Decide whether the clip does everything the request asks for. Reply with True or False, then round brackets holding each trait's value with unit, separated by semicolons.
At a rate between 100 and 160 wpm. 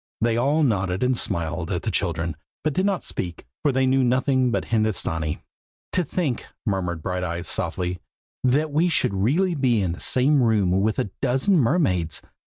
False (175 wpm)